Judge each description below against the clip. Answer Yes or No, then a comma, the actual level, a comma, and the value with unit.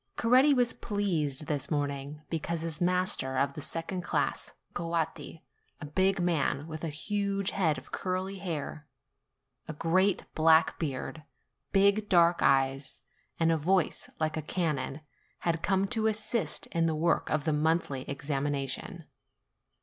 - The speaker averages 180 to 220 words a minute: No, average, 140 wpm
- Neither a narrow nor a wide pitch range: Yes, average, 4.1 semitones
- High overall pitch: No, medium, 165 Hz